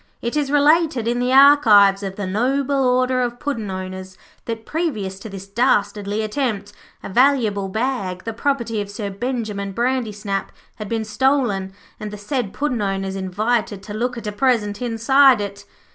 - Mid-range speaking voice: No, high, 220 Hz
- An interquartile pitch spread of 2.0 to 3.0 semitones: No, average, 4.2 semitones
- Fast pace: No, average, 165 wpm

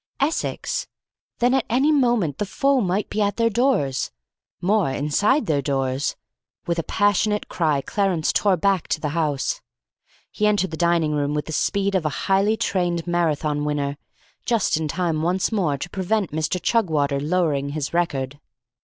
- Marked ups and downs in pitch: Yes, wide, 5.7 semitones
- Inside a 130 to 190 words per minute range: Yes, average, 165 wpm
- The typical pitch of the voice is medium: Yes, medium, 175 Hz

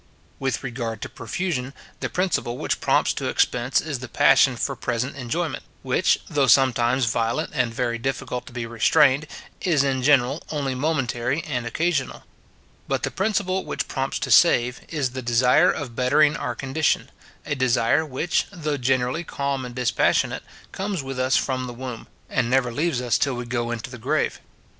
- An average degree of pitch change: Yes, average, 3.3 semitones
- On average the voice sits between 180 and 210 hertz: No, low, 130 Hz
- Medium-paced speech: Yes, average, 170 wpm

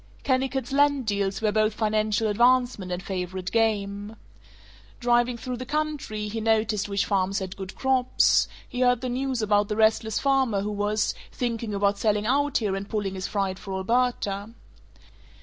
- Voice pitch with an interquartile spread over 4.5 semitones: No, average, 3.6 semitones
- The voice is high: Yes, high, 215 Hz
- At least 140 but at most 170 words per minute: Yes, average, 165 wpm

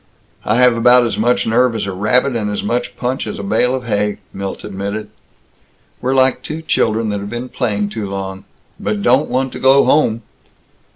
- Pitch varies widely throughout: No, average, 3.4 semitones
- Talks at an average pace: Yes, average, 195 wpm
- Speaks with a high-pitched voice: No, low, 115 Hz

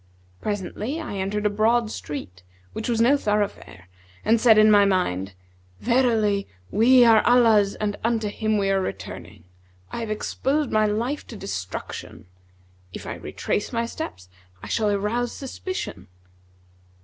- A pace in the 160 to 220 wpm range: No, average, 145 wpm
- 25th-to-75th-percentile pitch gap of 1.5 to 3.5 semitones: Yes, average, 2.8 semitones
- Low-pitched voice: No, high, 215 Hz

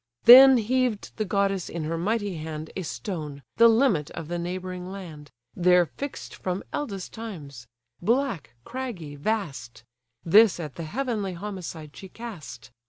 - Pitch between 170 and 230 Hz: Yes, medium, 185 Hz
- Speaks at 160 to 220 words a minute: No, average, 145 wpm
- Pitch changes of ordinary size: No, wide, 5.9 semitones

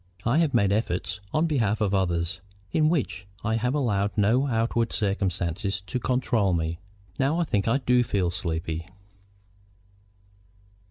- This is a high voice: No, low, 105 Hz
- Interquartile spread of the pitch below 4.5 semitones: No, average, 4.9 semitones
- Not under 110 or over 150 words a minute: Yes, average, 145 wpm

